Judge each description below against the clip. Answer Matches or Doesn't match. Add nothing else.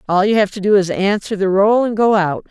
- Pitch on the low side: Doesn't match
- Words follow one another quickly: Matches